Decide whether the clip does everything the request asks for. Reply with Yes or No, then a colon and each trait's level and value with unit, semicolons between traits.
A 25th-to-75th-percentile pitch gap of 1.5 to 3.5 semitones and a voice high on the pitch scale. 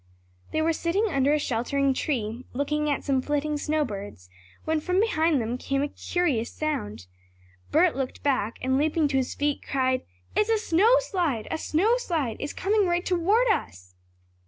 No: average, 4.8 semitones; very high, 295 Hz